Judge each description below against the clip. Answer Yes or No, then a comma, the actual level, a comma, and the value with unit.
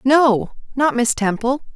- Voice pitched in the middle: No, very high, 255 Hz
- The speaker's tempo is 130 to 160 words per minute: Yes, slow, 135 wpm